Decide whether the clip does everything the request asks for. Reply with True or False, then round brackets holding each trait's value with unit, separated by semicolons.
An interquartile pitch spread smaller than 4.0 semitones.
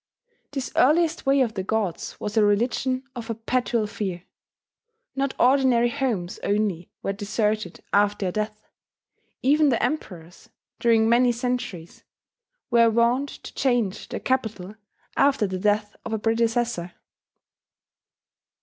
True (3.5 semitones)